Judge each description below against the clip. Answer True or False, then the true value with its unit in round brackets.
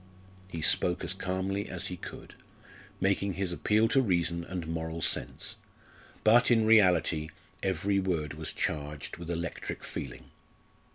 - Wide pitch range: False (3.0 semitones)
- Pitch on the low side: True (90 Hz)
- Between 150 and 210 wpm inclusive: False (135 wpm)